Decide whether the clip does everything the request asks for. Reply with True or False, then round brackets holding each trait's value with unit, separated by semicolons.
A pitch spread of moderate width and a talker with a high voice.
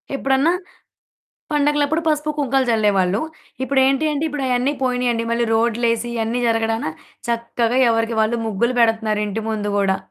True (3.2 semitones; 235 Hz)